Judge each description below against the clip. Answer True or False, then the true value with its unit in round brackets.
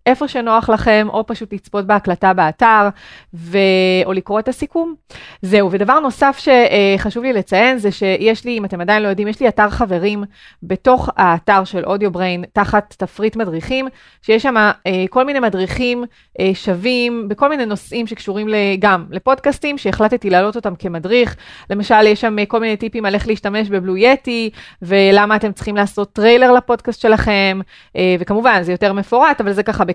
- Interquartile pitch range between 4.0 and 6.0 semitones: False (3.3 semitones)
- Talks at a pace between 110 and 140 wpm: False (150 wpm)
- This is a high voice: True (210 Hz)